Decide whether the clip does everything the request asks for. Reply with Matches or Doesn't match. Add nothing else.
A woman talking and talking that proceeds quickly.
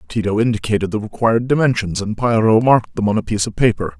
Doesn't match